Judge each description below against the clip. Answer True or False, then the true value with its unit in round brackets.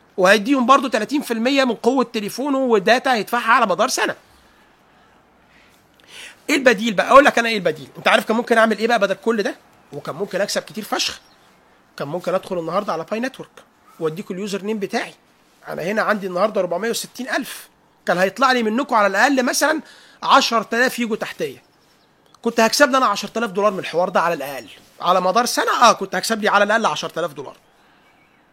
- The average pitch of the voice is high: True (225 Hz)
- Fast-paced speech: True (170 wpm)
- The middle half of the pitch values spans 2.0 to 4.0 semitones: False (4.4 semitones)